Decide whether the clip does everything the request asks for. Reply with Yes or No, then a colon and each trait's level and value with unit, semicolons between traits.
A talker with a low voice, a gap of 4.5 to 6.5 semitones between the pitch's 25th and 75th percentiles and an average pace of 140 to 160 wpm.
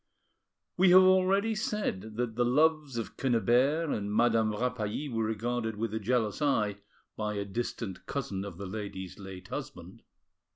Yes: low, 115 Hz; average, 5.1 semitones; average, 155 wpm